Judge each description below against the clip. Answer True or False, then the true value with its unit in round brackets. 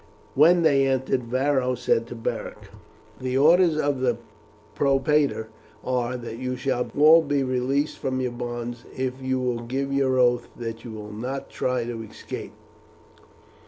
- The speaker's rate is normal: True (155 wpm)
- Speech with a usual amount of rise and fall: False (2.3 semitones)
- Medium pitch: False (130 Hz)